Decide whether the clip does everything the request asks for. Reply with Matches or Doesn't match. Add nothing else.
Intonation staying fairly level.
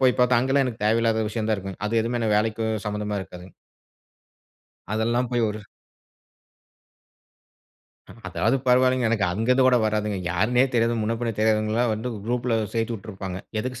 Matches